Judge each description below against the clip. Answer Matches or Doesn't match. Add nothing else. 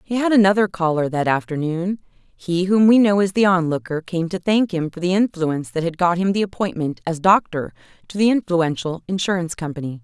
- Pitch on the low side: Doesn't match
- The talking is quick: Doesn't match